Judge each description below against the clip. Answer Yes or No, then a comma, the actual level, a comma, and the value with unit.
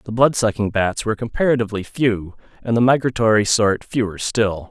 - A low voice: Yes, low, 110 Hz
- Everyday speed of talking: Yes, average, 165 wpm